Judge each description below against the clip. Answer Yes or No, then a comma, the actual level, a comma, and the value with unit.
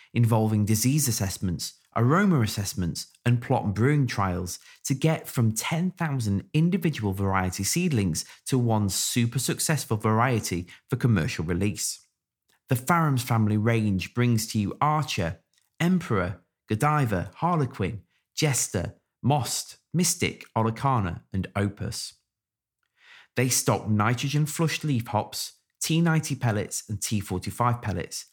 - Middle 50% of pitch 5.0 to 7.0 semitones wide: Yes, wide, 5.6 semitones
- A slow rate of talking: Yes, slow, 110 wpm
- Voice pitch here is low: Yes, low, 115 Hz